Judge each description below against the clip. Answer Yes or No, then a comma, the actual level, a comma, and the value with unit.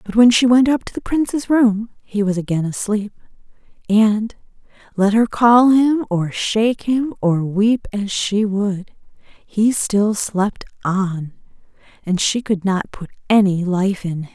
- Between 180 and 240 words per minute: No, average, 165 wpm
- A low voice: No, high, 210 Hz